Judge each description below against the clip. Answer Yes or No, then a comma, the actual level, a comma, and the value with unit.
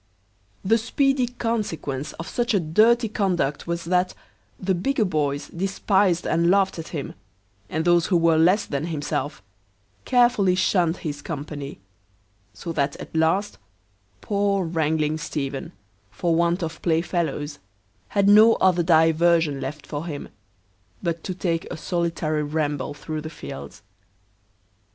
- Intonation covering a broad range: No, average, 3.8 semitones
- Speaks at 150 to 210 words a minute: No, slow, 135 wpm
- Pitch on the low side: No, medium, 170 Hz